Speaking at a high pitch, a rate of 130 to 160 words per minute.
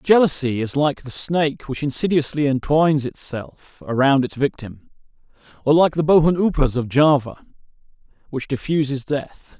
No: medium, 140 Hz; average, 140 wpm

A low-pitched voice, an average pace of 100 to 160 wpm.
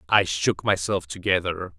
Yes: very low, 85 Hz; slow, 135 wpm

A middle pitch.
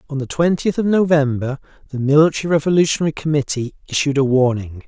Yes: medium, 145 Hz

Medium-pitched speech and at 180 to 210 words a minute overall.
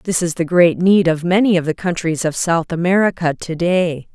Yes: medium, 170 Hz; fast, 205 wpm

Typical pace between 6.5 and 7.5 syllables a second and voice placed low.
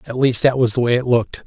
Yes: 6.6 syllables/s; low, 125 Hz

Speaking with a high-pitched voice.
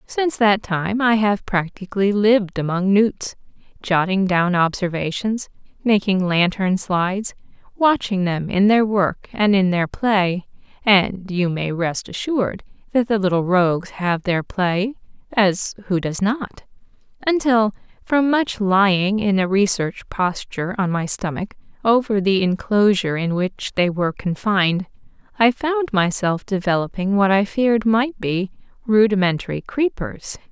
Yes: high, 200 Hz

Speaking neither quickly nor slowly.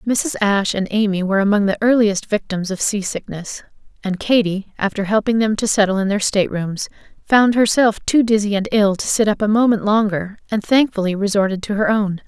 Yes: average, 195 wpm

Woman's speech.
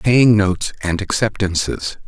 No: male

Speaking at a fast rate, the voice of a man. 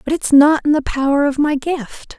No: fast, 245 wpm; female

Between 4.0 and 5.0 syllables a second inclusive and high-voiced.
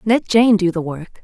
Yes: 4.5 syllables/s; high, 200 Hz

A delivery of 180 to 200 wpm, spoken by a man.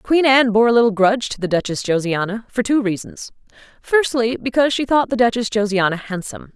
No: average, 190 wpm; female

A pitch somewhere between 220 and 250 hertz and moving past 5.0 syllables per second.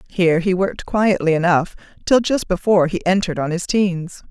No: medium, 185 Hz; 5.6 syllables/s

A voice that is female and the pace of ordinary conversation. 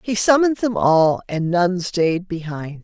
Yes: female; average, 170 wpm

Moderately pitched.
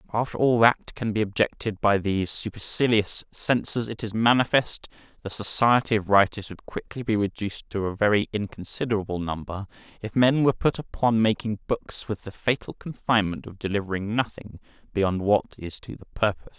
No: low, 105 Hz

